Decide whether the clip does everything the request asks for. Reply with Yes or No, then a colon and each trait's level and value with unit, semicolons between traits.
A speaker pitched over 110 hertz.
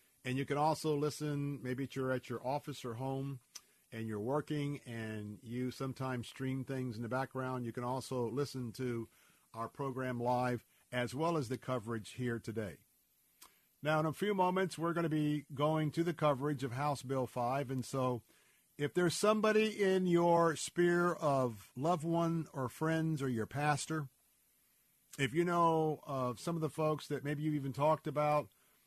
Yes: medium, 140 Hz